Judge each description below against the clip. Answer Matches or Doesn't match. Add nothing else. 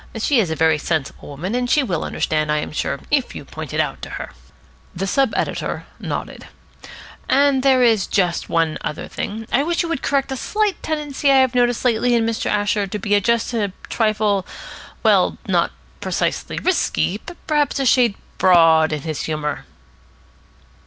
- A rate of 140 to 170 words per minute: Doesn't match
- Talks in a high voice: Matches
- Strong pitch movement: Matches